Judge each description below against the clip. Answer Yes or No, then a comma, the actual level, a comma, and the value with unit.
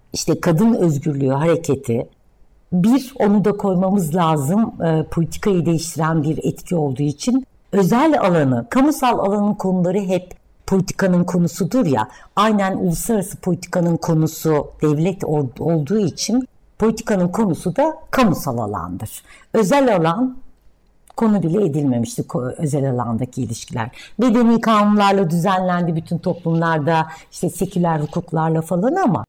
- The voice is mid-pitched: Yes, medium, 175 Hz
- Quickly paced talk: No, average, 115 wpm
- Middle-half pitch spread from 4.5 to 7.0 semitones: Yes, average, 5.0 semitones